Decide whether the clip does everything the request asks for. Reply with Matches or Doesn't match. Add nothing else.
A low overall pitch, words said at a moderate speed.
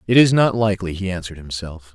Doesn't match